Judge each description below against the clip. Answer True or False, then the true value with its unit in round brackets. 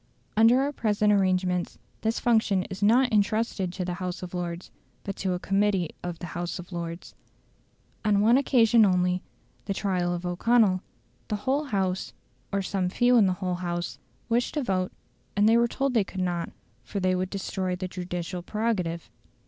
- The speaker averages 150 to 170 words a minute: False (180 wpm)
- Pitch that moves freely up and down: False (3.4 semitones)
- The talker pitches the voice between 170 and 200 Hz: True (190 Hz)